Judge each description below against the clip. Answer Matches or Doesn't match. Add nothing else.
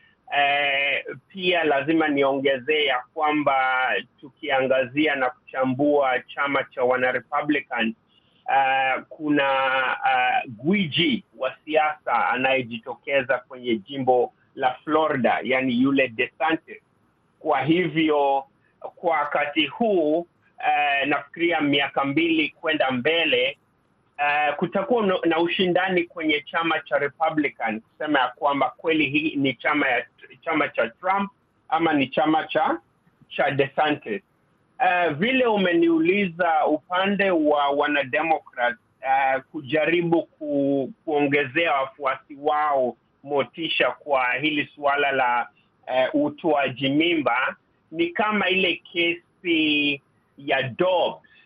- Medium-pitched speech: Matches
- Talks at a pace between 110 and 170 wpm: Doesn't match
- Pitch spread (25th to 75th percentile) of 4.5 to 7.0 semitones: Doesn't match